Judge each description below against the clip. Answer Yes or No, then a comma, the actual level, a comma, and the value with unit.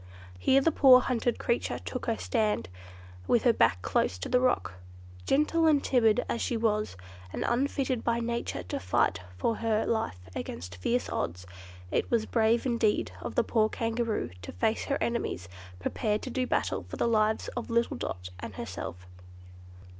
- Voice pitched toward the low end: No, high, 230 Hz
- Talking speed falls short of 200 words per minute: Yes, average, 170 wpm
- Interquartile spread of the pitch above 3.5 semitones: No, average, 3.0 semitones